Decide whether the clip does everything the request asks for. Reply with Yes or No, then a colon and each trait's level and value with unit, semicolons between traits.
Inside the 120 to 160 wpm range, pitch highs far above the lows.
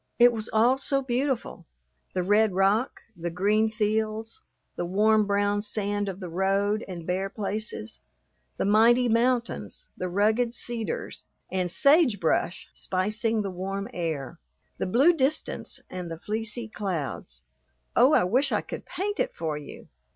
No: average, 150 wpm; average, 4.1 semitones